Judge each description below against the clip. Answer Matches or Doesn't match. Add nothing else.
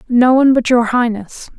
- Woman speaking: Matches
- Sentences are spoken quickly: Doesn't match